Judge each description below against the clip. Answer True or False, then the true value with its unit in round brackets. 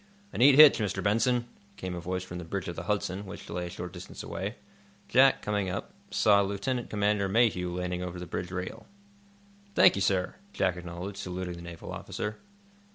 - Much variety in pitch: False (2.7 semitones)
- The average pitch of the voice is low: True (95 Hz)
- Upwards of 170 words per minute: True (190 wpm)